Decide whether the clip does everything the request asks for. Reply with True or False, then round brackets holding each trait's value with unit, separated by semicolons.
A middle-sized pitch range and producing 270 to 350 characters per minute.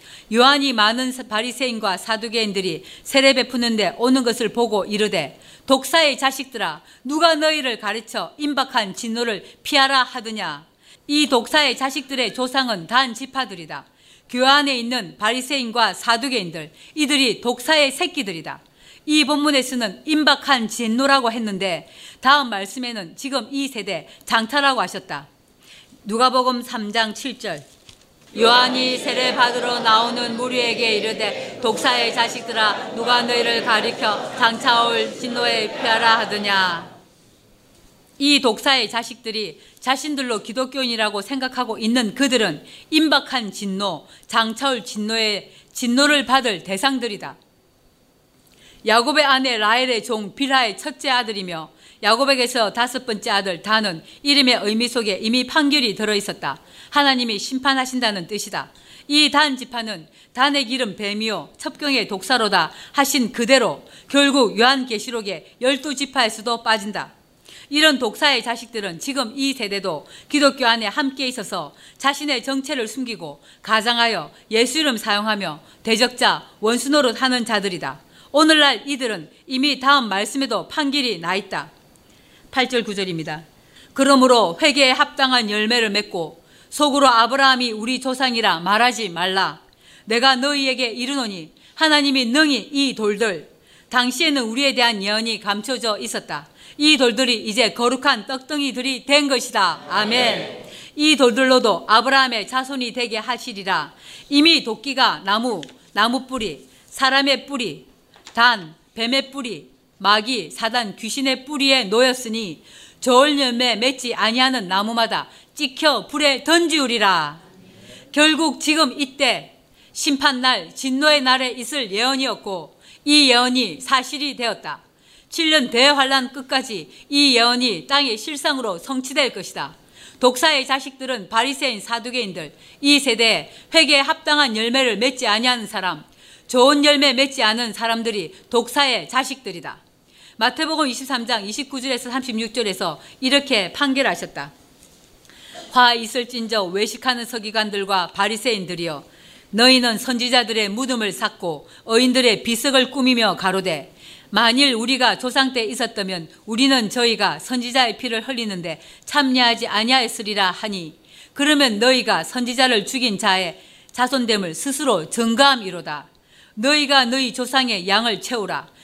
True (3.7 semitones; 300 characters per minute)